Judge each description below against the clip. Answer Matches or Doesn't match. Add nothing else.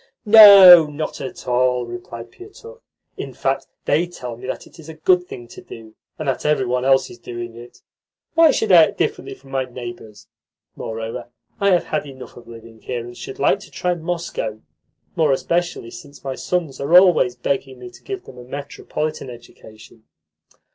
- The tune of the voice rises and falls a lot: Matches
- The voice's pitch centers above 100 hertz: Matches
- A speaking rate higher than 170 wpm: Matches